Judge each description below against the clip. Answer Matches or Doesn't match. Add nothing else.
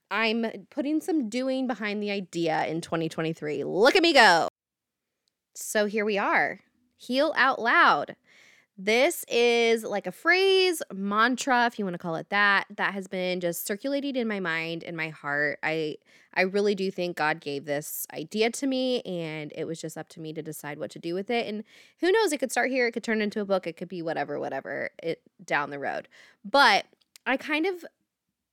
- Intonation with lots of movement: Matches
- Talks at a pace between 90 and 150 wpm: Doesn't match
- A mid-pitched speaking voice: Doesn't match